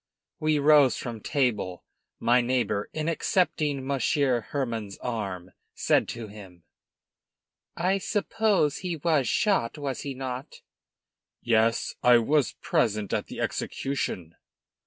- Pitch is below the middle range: Yes, low, 130 Hz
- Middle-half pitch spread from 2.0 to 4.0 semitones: No, average, 5.2 semitones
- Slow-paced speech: Yes, slow, 115 wpm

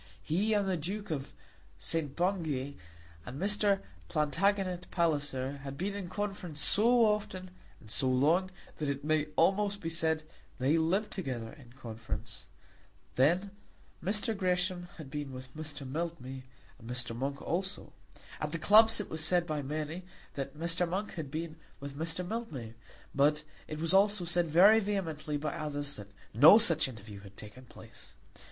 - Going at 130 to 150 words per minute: No, average, 160 wpm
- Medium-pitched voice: Yes, medium, 160 Hz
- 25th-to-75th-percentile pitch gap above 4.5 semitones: Yes, average, 5.2 semitones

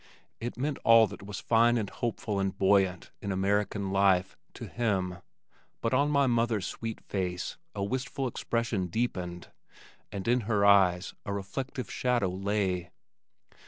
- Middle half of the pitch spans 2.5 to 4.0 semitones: Yes, average, 3.6 semitones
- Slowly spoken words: No, average, 150 wpm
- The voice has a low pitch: Yes, low, 100 Hz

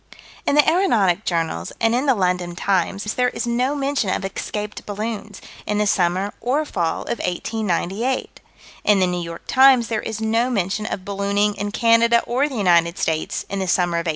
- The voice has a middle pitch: No, high, 210 Hz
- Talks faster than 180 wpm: Yes, average, 190 wpm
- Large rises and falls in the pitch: No, average, 4.5 semitones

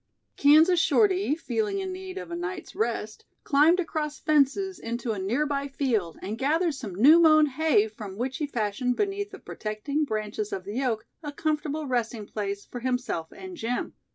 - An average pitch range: No, wide, 6.7 semitones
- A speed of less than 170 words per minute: No, average, 175 wpm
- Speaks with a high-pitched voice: Yes, very high, 280 Hz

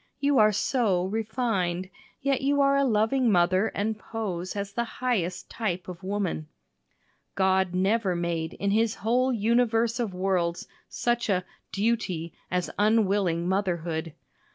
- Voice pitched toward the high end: Yes, high, 200 Hz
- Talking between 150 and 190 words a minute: No, slow, 135 wpm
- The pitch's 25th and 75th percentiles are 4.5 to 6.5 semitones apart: No, average, 4.1 semitones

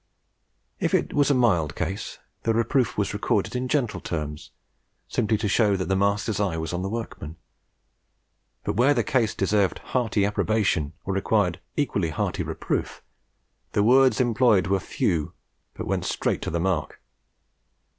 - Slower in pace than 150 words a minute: No, average, 155 wpm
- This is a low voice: Yes, low, 105 Hz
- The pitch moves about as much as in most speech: Yes, average, 4.1 semitones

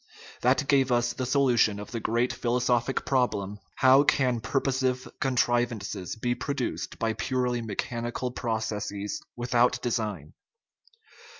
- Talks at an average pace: No, slow, 130 wpm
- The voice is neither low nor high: No, low, 120 Hz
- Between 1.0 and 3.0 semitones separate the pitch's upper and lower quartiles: Yes, narrow, 2.4 semitones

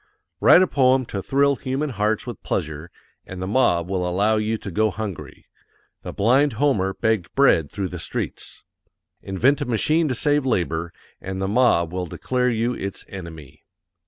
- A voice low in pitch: Yes, low, 105 Hz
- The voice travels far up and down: Yes, wide, 5.9 semitones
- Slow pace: No, average, 170 wpm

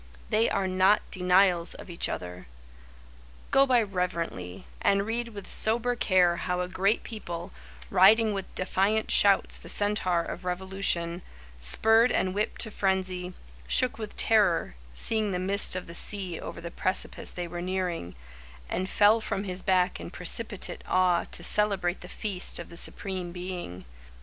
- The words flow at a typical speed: Yes, average, 155 wpm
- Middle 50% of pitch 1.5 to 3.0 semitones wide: Yes, narrow, 2.5 semitones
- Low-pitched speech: No, medium, 185 Hz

